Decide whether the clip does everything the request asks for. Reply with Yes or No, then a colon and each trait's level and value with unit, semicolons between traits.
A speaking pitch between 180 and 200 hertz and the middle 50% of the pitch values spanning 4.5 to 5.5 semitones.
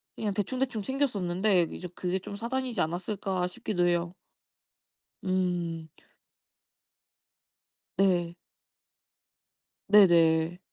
No: medium, 185 Hz; average, 3.2 semitones